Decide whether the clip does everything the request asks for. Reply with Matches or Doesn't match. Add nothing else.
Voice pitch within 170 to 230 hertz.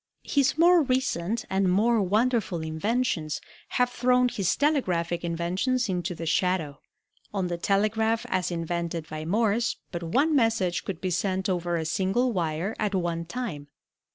Matches